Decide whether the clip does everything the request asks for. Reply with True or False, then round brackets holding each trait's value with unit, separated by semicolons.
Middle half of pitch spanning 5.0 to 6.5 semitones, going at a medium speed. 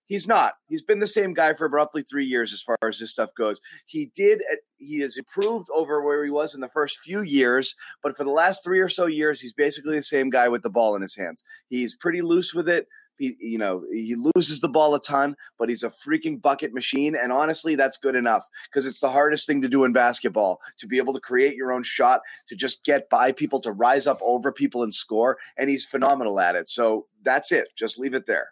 False (5.5 semitones; 245 wpm)